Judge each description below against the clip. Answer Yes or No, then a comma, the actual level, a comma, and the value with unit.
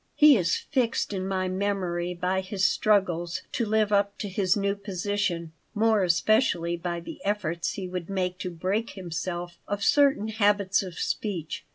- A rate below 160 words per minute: No, average, 165 wpm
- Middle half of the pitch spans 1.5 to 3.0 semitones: Yes, average, 2.7 semitones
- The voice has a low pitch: No, high, 190 Hz